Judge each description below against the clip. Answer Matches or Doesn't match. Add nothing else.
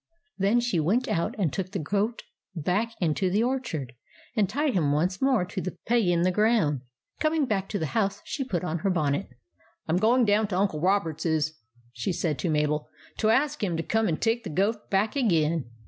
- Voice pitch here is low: Doesn't match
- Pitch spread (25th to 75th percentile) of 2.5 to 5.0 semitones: Doesn't match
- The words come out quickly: Matches